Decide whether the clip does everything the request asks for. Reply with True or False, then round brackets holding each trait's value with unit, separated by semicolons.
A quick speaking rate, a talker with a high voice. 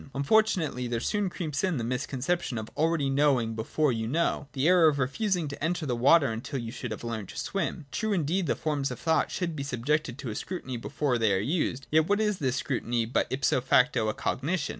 False (220 wpm; 140 Hz)